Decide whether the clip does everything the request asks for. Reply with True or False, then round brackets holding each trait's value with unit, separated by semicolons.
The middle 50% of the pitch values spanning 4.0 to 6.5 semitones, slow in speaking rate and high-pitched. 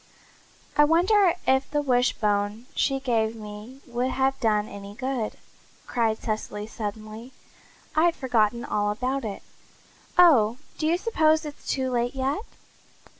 True (4.4 semitones; 130 wpm; 245 Hz)